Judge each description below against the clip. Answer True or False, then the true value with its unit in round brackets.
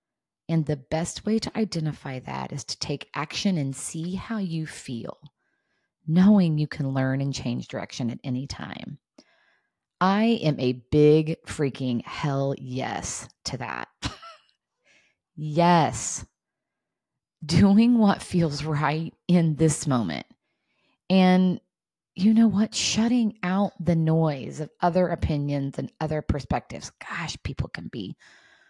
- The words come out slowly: True (130 wpm)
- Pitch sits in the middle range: True (160 Hz)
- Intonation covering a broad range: False (4.6 semitones)